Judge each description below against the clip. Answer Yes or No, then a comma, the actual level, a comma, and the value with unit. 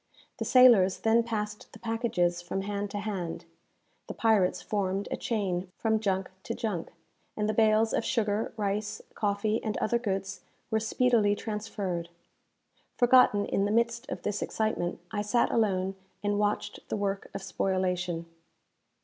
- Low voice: No, high, 205 Hz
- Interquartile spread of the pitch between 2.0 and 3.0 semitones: Yes, narrow, 2.4 semitones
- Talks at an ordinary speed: Yes, average, 150 wpm